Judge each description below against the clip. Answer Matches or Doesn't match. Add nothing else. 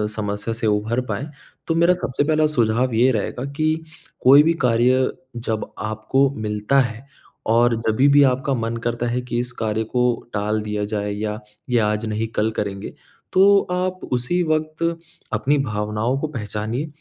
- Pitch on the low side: Matches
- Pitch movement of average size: Matches